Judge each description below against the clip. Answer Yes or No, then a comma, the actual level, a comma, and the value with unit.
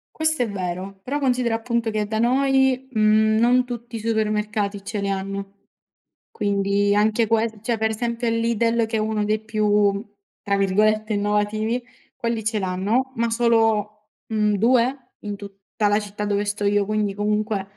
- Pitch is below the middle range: No, high, 215 Hz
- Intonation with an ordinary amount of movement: No, narrow, 2.1 semitones